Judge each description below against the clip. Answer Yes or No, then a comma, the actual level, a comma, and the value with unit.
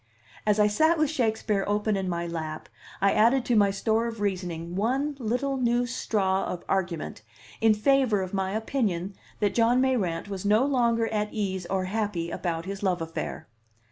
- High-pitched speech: Yes, high, 210 Hz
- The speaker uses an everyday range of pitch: Yes, average, 3.9 semitones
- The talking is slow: No, average, 175 wpm